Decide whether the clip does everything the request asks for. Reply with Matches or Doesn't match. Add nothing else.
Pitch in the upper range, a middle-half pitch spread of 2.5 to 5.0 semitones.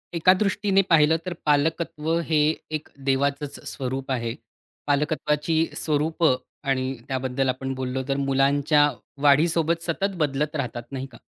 Doesn't match